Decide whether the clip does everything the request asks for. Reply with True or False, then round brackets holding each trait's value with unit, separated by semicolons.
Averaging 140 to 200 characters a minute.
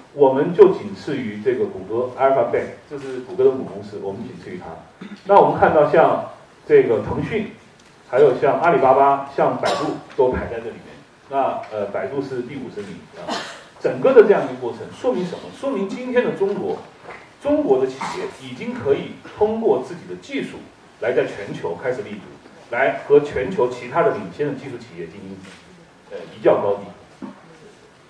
False (285 characters per minute)